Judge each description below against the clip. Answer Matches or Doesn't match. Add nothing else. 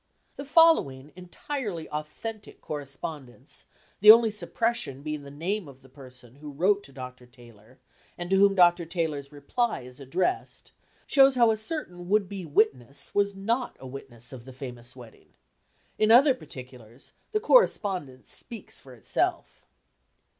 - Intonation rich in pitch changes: Matches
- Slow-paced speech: Doesn't match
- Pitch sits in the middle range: Matches